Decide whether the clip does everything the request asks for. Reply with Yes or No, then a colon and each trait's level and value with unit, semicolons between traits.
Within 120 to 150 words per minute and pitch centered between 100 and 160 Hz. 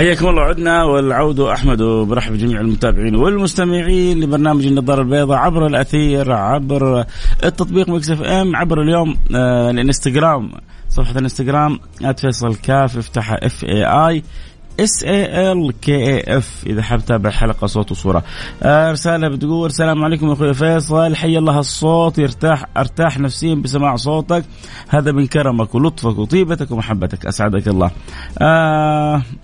Yes: average, 130 wpm; medium, 140 Hz